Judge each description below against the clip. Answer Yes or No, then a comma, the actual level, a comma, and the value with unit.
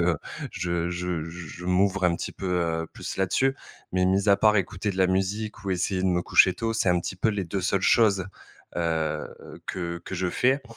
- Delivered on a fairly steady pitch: Yes, narrow, 2.3 semitones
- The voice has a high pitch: No, very low, 95 Hz